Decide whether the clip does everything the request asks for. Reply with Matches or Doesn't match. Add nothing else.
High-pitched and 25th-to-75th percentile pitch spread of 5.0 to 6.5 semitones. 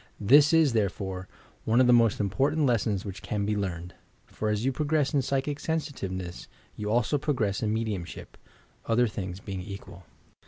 Doesn't match